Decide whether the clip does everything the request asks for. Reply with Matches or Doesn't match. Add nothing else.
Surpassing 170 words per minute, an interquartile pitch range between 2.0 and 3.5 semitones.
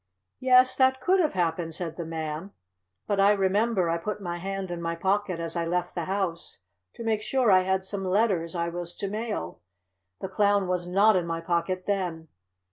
Matches